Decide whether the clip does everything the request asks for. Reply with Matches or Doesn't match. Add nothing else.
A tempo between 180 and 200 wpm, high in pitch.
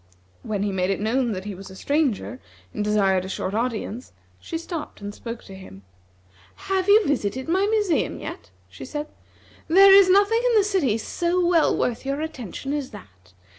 Matches